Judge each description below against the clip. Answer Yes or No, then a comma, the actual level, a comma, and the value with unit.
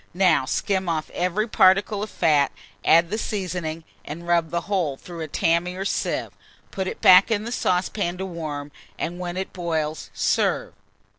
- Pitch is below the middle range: No, medium, 175 Hz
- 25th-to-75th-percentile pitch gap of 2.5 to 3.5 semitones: Yes, average, 2.8 semitones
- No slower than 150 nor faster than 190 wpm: Yes, average, 170 wpm